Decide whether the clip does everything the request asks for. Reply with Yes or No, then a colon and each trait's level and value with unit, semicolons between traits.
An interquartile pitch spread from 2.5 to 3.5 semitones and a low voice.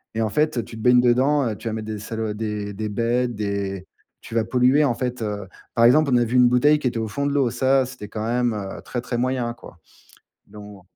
Yes: average, 2.8 semitones; low, 120 Hz